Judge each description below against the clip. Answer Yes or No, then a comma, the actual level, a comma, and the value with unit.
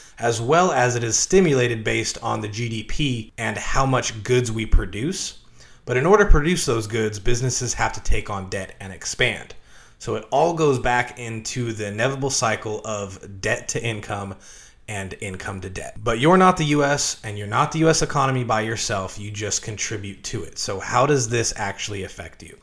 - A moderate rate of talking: Yes, average, 195 wpm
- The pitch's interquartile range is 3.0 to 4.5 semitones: Yes, average, 4.1 semitones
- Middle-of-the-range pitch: No, low, 115 Hz